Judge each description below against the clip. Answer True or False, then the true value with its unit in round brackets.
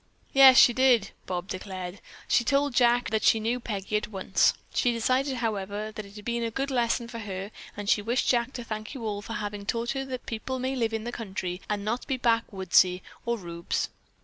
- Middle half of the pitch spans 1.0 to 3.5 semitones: True (3.2 semitones)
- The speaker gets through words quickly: True (215 wpm)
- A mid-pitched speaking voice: False (225 Hz)